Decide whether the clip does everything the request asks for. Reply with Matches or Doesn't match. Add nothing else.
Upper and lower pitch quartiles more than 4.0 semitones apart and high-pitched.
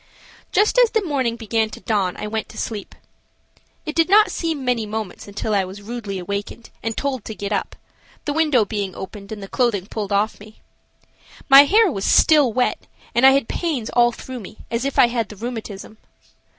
Matches